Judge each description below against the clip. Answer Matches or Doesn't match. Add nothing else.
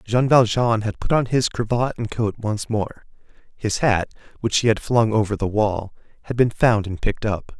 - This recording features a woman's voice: Doesn't match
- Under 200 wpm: Doesn't match